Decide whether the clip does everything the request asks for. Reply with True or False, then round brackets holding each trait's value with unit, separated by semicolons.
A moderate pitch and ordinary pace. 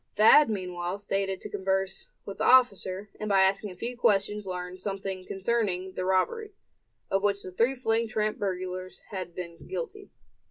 False (195 Hz; 165 wpm)